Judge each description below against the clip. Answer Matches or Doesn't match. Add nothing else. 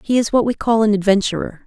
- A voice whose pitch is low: Doesn't match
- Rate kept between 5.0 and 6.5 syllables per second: Matches